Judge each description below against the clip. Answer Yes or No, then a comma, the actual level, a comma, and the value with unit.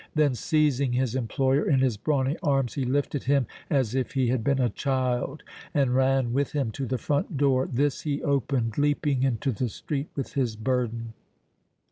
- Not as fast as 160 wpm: No, average, 180 wpm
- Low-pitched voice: Yes, low, 130 Hz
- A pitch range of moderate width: No, narrow, 2.2 semitones